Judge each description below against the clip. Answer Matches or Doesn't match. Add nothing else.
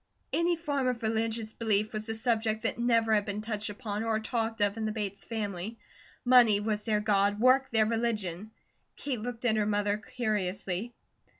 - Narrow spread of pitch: Matches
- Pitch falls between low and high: Doesn't match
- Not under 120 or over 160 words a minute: Doesn't match